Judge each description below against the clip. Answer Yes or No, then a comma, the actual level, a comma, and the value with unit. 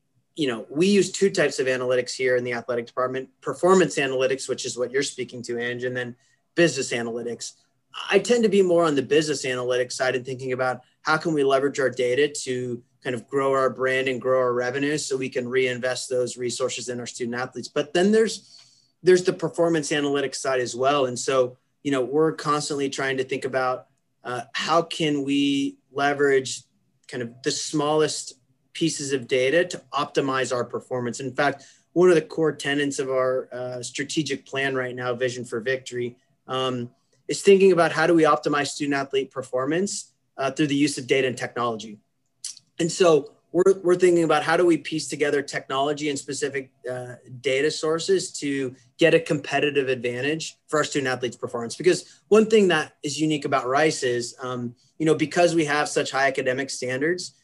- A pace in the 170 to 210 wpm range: Yes, average, 190 wpm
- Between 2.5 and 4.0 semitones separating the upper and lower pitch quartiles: Yes, average, 3.2 semitones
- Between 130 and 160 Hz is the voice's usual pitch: Yes, low, 135 Hz